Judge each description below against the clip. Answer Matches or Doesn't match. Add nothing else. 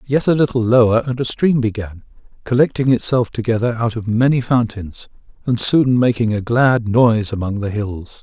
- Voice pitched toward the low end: Matches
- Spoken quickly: Doesn't match